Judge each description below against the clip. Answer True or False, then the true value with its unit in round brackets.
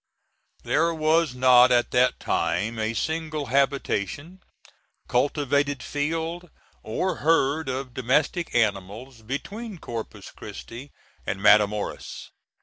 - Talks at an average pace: False (100 wpm)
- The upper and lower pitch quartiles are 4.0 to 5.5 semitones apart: True (5.1 semitones)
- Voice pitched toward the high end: False (135 Hz)